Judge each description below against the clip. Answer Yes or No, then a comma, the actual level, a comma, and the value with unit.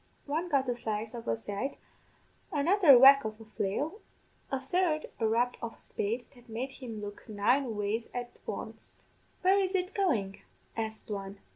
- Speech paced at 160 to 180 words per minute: Yes, average, 175 wpm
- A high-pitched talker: Yes, high, 245 Hz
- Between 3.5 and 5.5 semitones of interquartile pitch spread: Yes, average, 4.7 semitones